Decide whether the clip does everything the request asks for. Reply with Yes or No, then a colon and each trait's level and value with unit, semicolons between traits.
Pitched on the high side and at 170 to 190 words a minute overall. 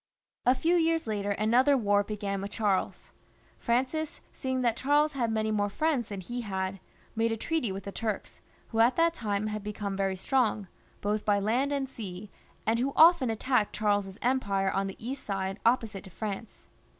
Yes: high, 220 Hz; average, 185 wpm